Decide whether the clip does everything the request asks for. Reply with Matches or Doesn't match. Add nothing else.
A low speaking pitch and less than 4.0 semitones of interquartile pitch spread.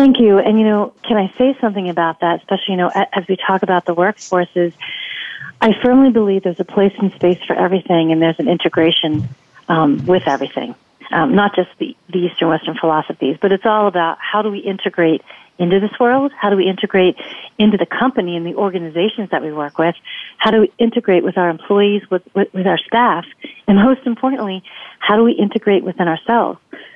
Doesn't match